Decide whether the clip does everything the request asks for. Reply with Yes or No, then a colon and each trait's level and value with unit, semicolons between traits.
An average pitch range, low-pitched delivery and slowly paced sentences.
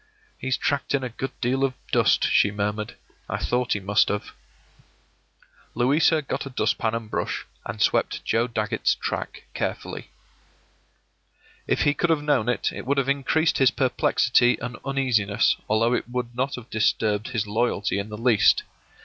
No: average, 3.7 semitones; low, 120 Hz; average, 165 wpm